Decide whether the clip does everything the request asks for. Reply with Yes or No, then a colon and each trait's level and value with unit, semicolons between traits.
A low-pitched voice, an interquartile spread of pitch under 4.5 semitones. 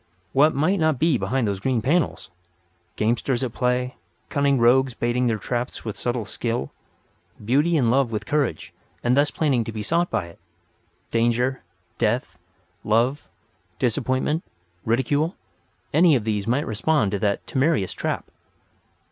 Yes: low, 125 Hz; average, 4.0 semitones